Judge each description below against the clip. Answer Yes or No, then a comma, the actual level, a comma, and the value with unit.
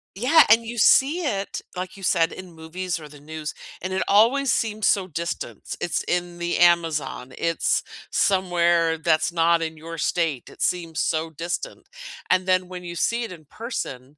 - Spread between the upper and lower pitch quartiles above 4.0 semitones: No, average, 3.0 semitones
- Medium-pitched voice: Yes, medium, 175 Hz